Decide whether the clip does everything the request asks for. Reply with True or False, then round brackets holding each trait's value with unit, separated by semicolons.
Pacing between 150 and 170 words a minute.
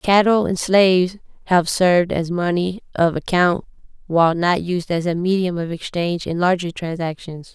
True (160 wpm)